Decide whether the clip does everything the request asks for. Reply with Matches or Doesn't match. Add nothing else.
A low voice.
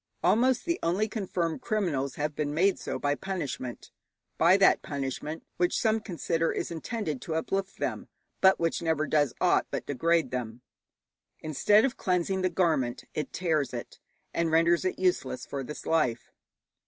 Doesn't match